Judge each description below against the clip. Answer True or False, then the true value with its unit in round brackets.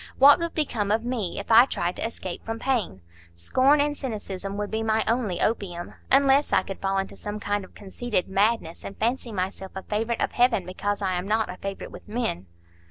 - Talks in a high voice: True (210 Hz)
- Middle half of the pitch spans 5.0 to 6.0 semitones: False (3.9 semitones)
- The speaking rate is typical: False (210 wpm)